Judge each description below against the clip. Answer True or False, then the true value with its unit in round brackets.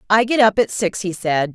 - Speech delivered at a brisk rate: True (270 wpm)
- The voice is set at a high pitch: True (200 Hz)